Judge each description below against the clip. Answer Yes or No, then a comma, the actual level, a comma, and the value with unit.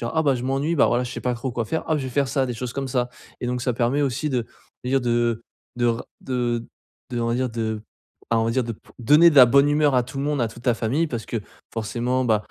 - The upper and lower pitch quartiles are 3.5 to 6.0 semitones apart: No, narrow, 2.5 semitones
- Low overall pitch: Yes, low, 125 Hz